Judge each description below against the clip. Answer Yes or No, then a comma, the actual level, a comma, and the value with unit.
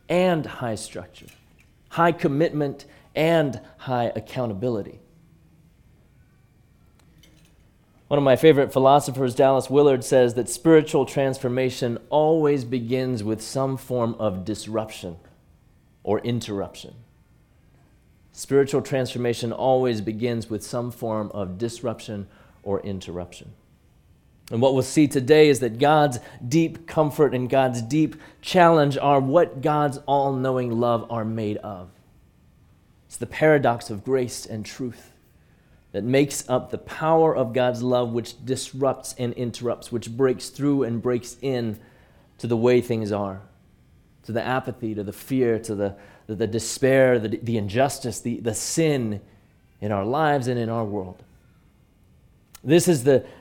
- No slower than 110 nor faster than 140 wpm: Yes, slow, 135 wpm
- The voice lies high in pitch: No, low, 125 Hz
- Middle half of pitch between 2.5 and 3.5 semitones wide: No, average, 3.9 semitones